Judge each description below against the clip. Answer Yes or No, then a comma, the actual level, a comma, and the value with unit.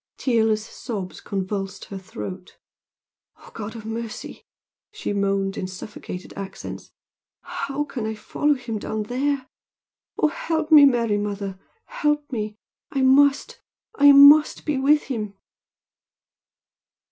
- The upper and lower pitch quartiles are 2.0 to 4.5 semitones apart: No, wide, 5.6 semitones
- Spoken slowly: Yes, slow, 125 wpm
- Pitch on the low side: No, high, 225 Hz